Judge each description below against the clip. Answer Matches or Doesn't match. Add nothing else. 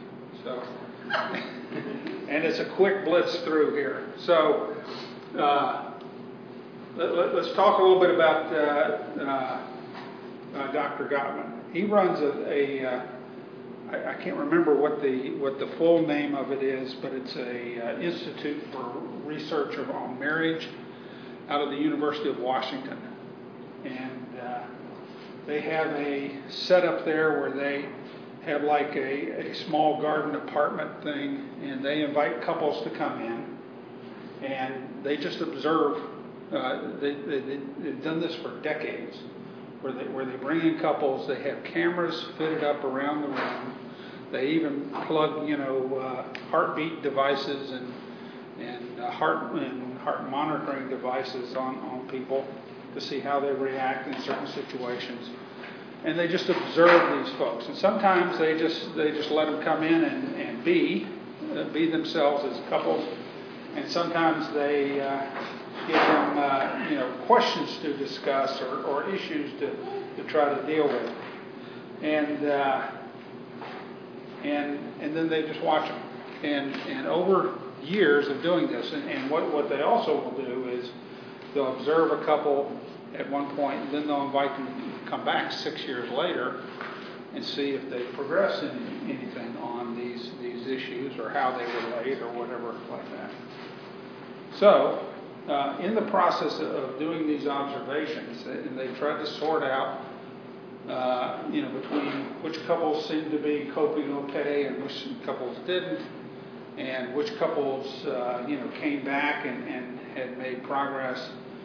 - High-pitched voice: Doesn't match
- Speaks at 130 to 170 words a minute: Matches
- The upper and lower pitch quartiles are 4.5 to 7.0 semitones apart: Doesn't match